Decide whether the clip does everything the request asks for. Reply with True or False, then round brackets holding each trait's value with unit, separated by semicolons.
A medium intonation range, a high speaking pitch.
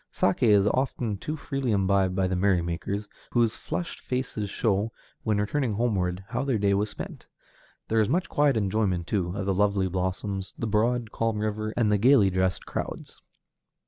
False (3.2 semitones; 105 Hz)